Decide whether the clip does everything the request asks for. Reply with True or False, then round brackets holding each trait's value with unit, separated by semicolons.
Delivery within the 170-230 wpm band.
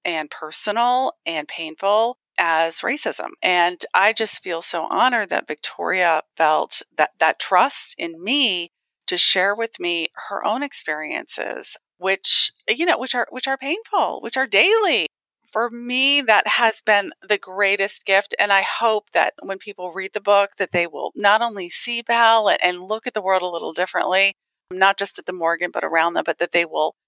True (180 wpm)